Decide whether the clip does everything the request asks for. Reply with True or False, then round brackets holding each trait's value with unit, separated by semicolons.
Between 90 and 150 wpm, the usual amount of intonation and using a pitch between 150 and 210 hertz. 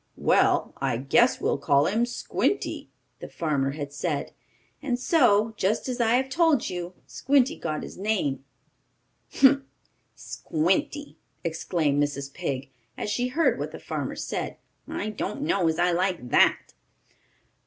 False (145 wpm; 8.8 semitones; 190 Hz)